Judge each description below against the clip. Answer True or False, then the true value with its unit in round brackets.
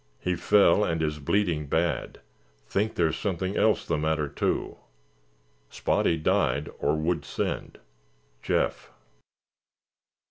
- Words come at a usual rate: False (110 wpm)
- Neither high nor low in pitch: False (80 Hz)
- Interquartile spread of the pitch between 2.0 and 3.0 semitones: False (3.5 semitones)